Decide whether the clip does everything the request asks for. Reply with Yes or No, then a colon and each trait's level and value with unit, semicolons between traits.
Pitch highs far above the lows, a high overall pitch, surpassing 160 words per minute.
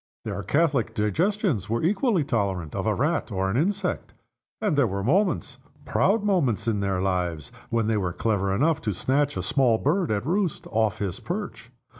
No: wide, 8.8 semitones; low, 115 Hz; average, 180 wpm